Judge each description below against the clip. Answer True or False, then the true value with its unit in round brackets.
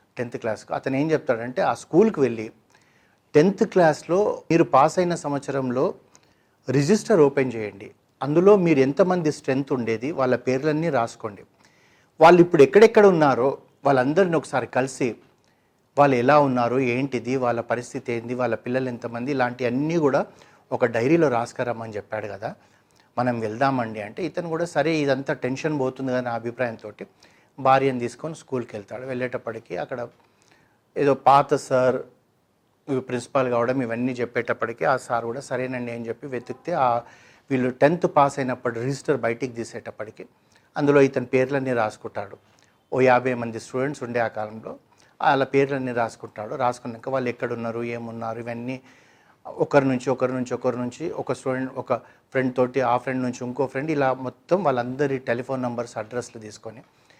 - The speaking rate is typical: False (135 wpm)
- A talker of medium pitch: False (130 Hz)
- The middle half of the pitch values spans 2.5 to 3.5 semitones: True (2.8 semitones)